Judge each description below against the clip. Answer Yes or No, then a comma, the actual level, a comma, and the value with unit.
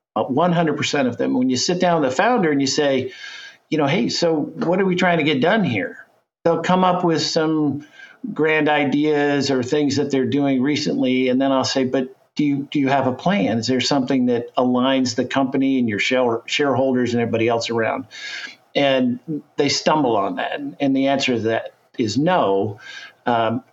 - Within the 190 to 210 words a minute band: Yes, average, 200 wpm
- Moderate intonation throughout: Yes, average, 3.3 semitones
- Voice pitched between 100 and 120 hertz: No, medium, 140 Hz